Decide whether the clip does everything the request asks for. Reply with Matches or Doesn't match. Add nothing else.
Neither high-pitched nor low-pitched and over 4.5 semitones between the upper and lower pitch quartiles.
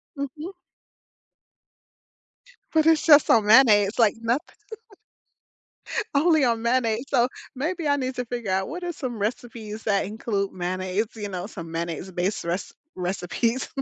Doesn't match